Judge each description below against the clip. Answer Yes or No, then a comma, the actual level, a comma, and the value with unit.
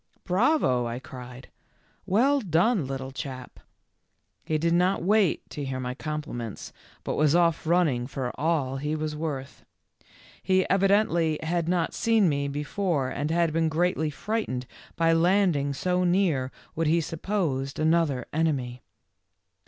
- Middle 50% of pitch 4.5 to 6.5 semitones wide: Yes, average, 4.8 semitones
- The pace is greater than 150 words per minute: No, average, 145 wpm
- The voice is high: No, medium, 160 Hz